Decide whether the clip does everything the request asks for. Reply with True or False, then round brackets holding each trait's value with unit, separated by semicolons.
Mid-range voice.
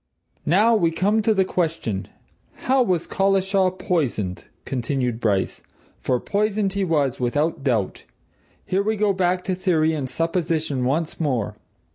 True (165 Hz)